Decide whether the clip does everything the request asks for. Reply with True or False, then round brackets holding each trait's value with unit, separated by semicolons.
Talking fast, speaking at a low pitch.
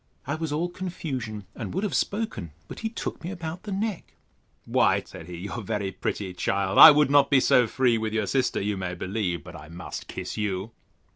True (215 wpm; 115 Hz)